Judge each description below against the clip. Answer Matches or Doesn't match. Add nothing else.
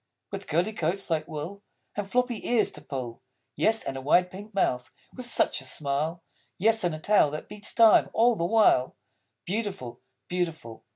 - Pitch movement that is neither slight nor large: Doesn't match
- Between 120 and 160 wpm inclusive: Doesn't match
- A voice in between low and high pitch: Matches